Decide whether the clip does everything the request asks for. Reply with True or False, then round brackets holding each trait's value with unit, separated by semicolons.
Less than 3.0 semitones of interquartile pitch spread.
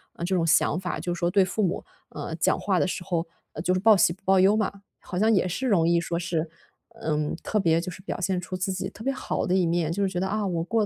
True (2.4 semitones)